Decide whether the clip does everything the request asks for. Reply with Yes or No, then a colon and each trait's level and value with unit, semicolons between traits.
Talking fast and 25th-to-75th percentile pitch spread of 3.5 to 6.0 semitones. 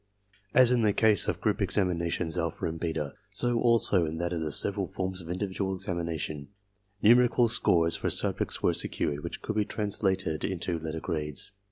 No: average, 175 wpm; average, 4.3 semitones